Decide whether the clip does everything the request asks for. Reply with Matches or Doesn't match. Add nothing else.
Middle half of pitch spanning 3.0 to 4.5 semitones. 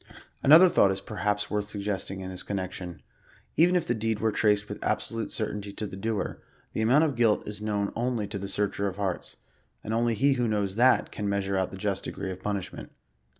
Doesn't match